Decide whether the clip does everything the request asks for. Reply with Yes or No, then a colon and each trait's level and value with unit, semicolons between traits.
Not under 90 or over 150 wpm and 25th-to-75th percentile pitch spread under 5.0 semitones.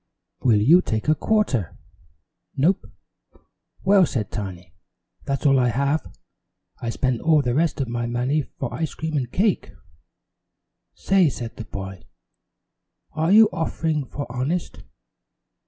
No: slow, 135 wpm; wide, 5.4 semitones